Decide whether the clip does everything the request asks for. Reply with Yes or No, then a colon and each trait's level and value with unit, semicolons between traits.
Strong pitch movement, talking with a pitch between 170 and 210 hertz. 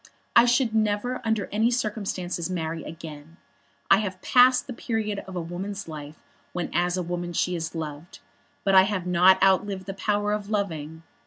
No: average, 3.6 semitones; high, 190 Hz